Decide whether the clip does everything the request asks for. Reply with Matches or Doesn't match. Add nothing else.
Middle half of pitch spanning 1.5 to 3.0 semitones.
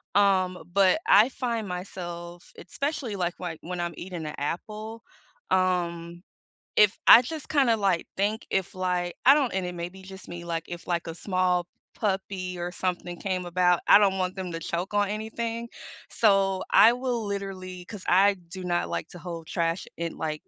Matches